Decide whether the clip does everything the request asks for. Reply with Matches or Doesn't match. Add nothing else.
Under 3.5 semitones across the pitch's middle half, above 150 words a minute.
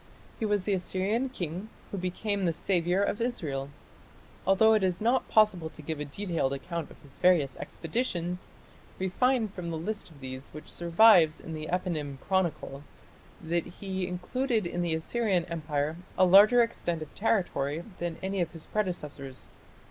Doesn't match